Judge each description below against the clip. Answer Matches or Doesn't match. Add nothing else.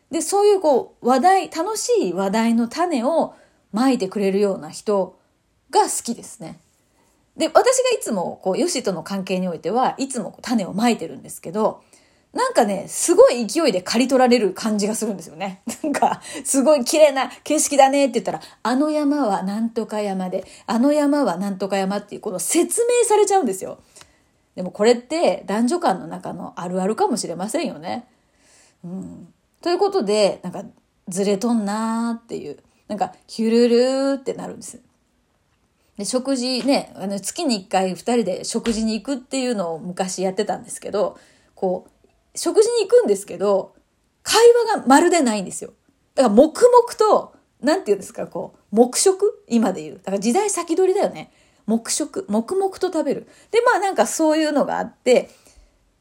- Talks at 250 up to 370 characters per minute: Matches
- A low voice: Doesn't match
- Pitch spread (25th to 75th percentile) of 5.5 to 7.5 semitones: Doesn't match